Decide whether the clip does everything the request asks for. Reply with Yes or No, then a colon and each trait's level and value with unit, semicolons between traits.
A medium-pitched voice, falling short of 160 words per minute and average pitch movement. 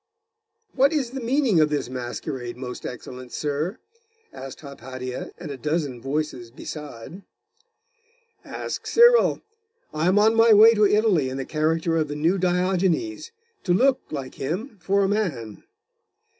No: medium, 160 Hz; average, 145 wpm; wide, 7.7 semitones